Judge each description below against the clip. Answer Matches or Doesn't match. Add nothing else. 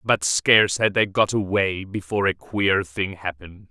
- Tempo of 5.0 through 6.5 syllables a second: Doesn't match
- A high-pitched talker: Doesn't match